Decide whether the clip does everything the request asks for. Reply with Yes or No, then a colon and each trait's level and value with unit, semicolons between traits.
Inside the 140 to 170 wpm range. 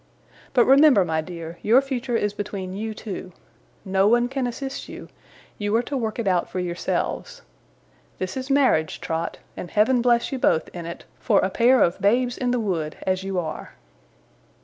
No: average, 185 wpm